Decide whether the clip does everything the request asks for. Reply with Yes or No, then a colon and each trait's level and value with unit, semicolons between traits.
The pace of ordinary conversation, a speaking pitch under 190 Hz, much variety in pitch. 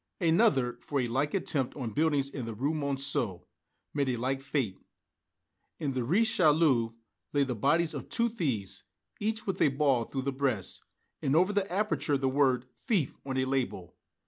No: average, 175 wpm; medium, 140 Hz; average, 3.8 semitones